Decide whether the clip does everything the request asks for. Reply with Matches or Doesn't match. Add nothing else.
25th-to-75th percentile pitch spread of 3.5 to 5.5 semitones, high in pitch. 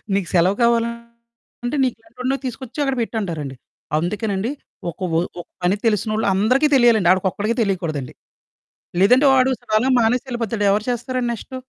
Matches